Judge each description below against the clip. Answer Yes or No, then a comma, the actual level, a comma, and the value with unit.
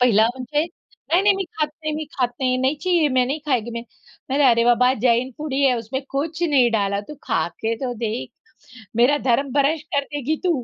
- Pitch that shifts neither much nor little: Yes, average, 4.0 semitones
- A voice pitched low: No, very high, 265 Hz